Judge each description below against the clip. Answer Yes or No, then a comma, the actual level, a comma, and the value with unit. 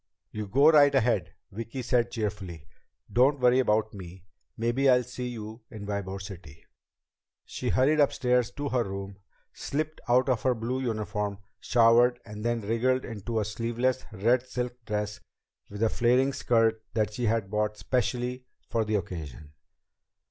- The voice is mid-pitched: No, low, 115 Hz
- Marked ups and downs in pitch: No, average, 3.1 semitones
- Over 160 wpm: No, average, 155 wpm